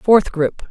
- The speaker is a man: No, female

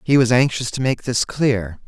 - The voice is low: Yes, low, 120 Hz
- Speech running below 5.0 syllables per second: Yes, 4.6 syllables/s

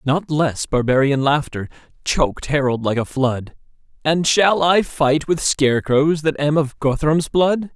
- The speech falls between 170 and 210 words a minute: No, average, 155 wpm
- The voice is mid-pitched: Yes, medium, 145 Hz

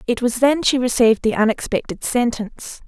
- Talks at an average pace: Yes, average, 165 wpm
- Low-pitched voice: No, high, 240 Hz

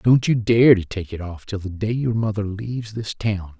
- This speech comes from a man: Yes, male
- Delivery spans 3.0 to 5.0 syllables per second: Yes, 4.9 syllables/s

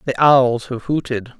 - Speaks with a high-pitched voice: No, low, 130 Hz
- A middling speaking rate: Yes, average, 170 wpm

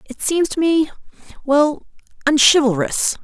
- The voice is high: Yes, very high, 285 Hz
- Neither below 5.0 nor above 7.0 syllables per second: No, 4.2 syllables/s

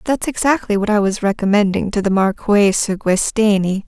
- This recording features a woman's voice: Yes, female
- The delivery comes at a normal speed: Yes, average, 170 wpm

